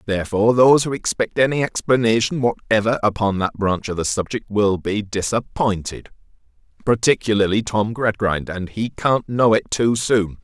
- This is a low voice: Yes, low, 110 Hz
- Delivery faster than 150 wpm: No, average, 145 wpm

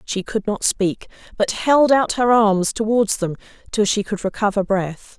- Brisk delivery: No, average, 185 wpm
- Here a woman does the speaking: Yes, female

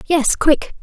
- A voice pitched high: Yes, very high, 295 Hz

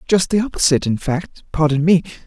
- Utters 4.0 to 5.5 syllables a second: No, 5.9 syllables/s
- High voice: No, medium, 160 Hz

